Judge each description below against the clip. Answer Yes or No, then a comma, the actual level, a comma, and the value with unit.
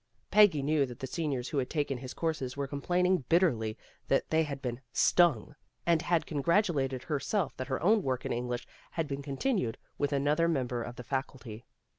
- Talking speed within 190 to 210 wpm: Yes, fast, 205 wpm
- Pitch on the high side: No, medium, 140 Hz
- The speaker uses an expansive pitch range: No, average, 4.5 semitones